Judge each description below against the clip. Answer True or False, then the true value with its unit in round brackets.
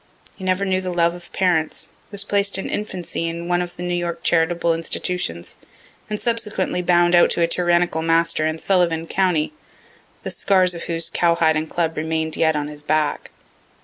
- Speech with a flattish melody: True (2.0 semitones)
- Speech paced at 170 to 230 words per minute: True (180 wpm)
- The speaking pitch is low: False (170 Hz)